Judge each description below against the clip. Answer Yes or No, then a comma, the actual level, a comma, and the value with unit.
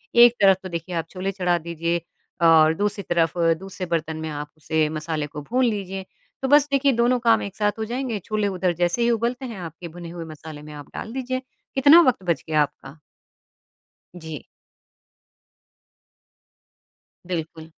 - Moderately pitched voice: Yes, medium, 180 Hz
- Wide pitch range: Yes, wide, 6.1 semitones